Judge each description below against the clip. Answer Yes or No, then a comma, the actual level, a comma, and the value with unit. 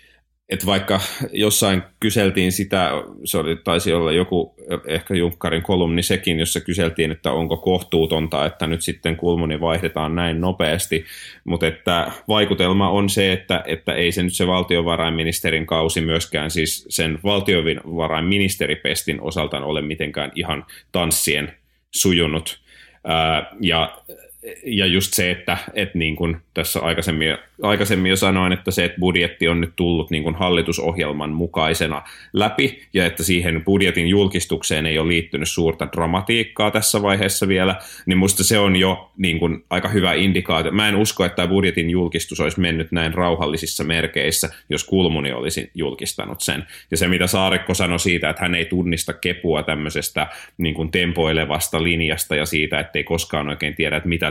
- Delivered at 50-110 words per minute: No, average, 150 wpm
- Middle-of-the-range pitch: No, very low, 85 Hz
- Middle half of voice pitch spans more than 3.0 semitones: No, average, 2.7 semitones